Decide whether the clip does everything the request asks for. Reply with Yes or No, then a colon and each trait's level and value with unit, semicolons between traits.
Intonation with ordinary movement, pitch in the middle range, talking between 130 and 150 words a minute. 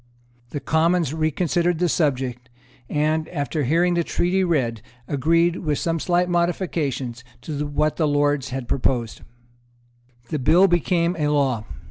Yes: average, 3.9 semitones; medium, 155 Hz; slow, 135 wpm